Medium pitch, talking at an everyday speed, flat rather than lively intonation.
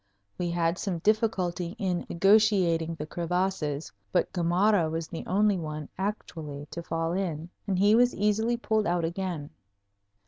No: medium, 175 Hz; average, 145 wpm; average, 3.6 semitones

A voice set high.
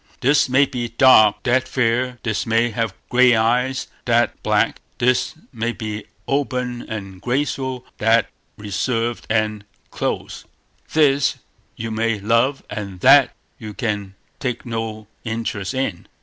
No: low, 115 Hz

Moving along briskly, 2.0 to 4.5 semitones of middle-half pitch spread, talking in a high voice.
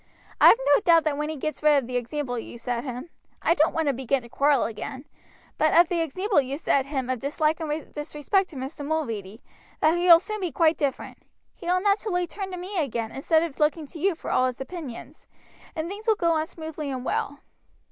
Yes: fast, 230 wpm; average, 4.1 semitones; very high, 305 Hz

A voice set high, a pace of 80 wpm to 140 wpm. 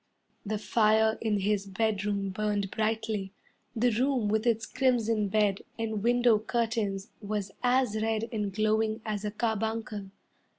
Yes: high, 215 Hz; slow, 135 wpm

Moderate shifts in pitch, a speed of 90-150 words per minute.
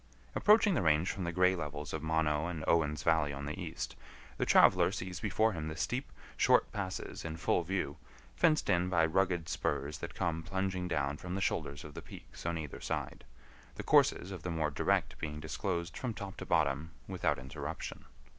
No: average, 3.4 semitones; average, 195 wpm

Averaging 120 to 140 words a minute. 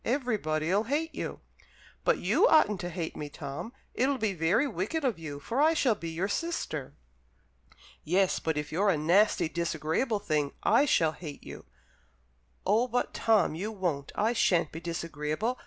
No: average, 165 wpm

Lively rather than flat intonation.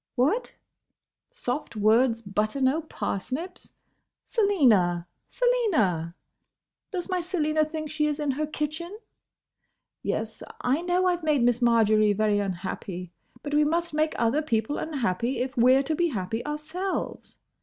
Yes: wide, 6.5 semitones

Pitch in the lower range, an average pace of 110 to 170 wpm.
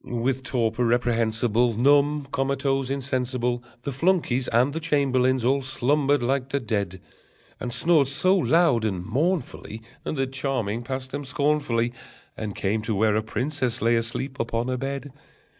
Yes: low, 130 Hz; average, 150 wpm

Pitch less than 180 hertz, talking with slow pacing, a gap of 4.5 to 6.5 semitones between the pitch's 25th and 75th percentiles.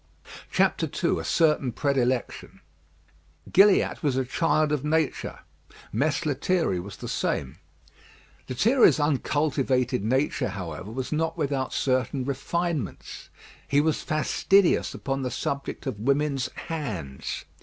No: medium, 140 Hz; slow, 110 wpm; average, 3.5 semitones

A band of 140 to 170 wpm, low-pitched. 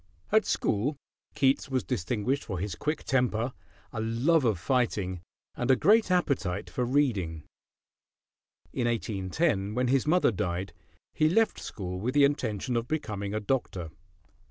Yes: average, 145 wpm; low, 120 Hz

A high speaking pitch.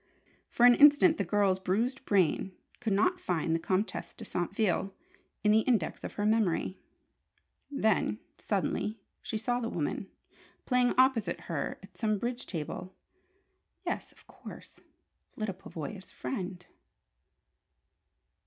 Yes: high, 210 Hz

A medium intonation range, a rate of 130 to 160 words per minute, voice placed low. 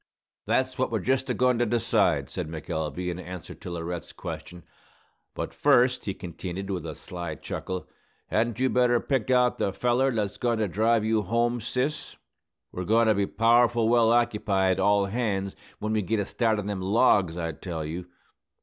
No: average, 4.6 semitones; average, 185 wpm; low, 105 Hz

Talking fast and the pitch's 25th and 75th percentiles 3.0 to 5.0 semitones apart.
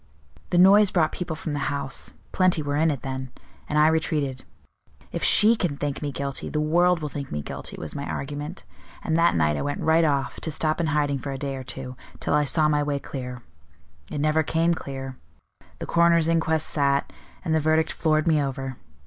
No: fast, 210 wpm; narrow, 2.6 semitones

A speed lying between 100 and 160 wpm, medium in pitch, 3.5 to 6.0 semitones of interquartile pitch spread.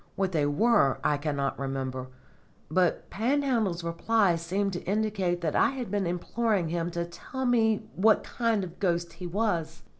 No: average, 170 wpm; medium, 180 Hz; average, 4.7 semitones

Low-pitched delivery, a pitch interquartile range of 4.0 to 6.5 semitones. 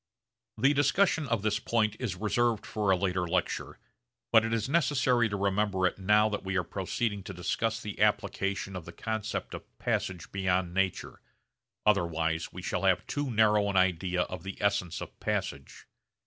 No: low, 100 Hz; average, 3.3 semitones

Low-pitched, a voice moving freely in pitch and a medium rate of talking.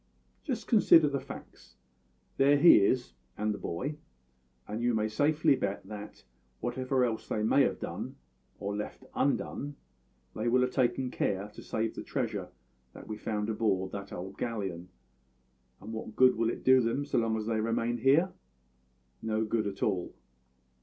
No: low, 115 Hz; average, 3.6 semitones; average, 165 wpm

